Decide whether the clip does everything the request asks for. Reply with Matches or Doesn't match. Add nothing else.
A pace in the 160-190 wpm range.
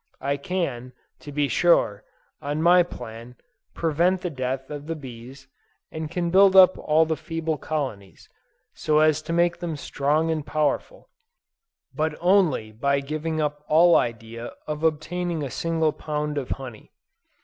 Doesn't match